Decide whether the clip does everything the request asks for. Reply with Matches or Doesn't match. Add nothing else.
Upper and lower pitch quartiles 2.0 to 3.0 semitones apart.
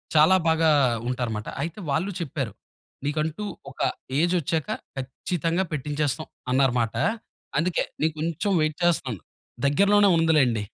Doesn't match